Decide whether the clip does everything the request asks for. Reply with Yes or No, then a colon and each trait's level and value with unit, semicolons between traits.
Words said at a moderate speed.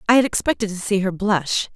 No: fast, 240 wpm